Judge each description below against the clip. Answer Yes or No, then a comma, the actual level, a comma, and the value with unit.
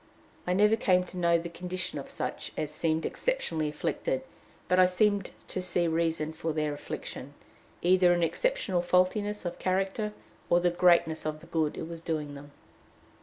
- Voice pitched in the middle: Yes, medium, 175 Hz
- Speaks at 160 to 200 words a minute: Yes, average, 170 wpm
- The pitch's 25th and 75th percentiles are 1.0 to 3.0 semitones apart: Yes, narrow, 2.5 semitones